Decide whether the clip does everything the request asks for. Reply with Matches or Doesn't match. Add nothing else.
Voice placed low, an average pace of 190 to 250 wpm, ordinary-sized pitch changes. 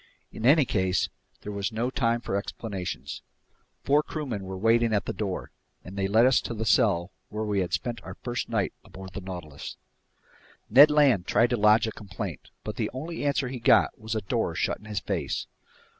Matches